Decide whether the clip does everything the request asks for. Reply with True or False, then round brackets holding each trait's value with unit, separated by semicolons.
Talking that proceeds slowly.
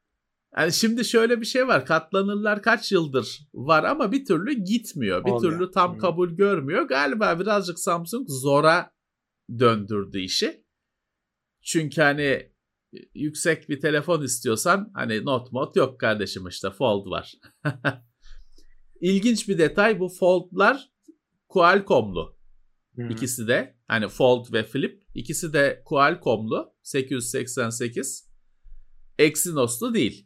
False (115 wpm)